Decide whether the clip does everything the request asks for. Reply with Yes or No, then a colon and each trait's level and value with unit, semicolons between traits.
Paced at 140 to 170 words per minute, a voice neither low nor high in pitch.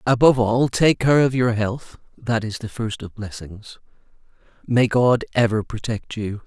No: average, 165 wpm; low, 115 Hz